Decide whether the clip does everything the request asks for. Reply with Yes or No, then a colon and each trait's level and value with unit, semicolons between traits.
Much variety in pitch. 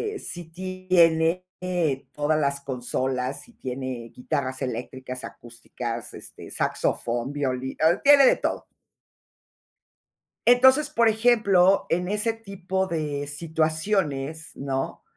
Yes: wide, 6.1 semitones